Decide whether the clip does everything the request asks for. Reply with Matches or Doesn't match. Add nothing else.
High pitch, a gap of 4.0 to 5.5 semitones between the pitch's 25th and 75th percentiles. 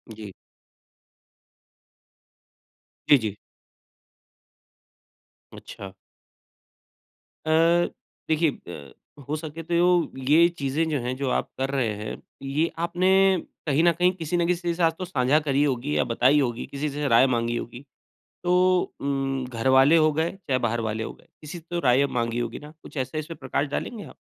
Doesn't match